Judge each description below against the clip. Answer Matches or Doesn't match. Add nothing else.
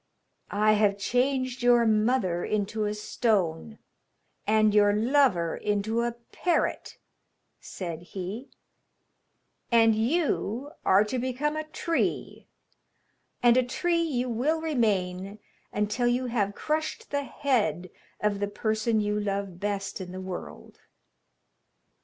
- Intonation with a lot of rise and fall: Doesn't match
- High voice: Matches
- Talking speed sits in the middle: Doesn't match